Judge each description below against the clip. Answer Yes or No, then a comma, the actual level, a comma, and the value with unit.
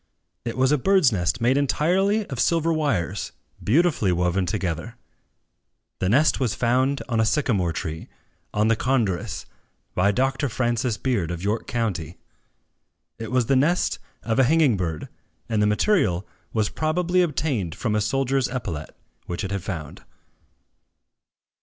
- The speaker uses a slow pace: No, average, 145 wpm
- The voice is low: Yes, low, 115 Hz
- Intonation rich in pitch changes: Yes, wide, 6.0 semitones